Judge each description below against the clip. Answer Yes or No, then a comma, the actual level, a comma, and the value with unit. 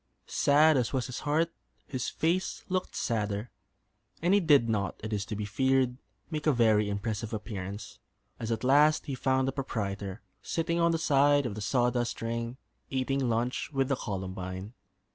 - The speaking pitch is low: Yes, low, 125 Hz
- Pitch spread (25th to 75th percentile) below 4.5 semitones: No, average, 5.1 semitones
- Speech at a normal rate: Yes, average, 170 wpm